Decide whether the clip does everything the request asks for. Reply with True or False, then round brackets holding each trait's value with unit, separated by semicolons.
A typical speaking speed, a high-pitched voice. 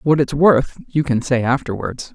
False (195 wpm; 135 Hz)